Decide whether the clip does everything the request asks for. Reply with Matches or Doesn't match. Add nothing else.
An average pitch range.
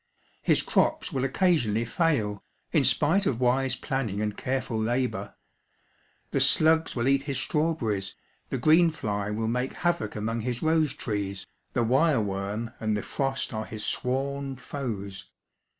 Matches